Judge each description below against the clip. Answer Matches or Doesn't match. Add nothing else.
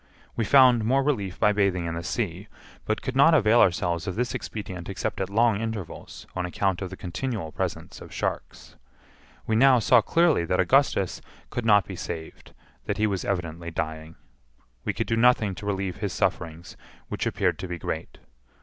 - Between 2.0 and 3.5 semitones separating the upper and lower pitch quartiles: Doesn't match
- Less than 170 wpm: Doesn't match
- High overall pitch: Doesn't match